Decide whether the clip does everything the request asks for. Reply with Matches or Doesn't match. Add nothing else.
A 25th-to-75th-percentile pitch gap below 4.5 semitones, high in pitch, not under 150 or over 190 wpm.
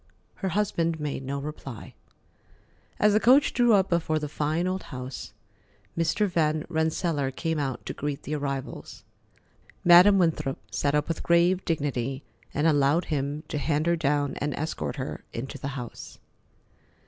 Doesn't match